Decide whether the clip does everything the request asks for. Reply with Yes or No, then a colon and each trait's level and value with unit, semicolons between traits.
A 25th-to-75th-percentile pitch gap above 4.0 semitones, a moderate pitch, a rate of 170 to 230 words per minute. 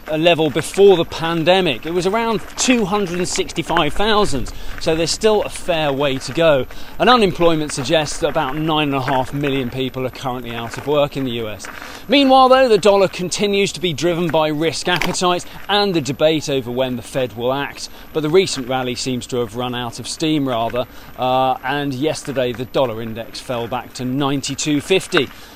Yes: wide, 5.6 semitones; medium, 150 Hz; average, 200 wpm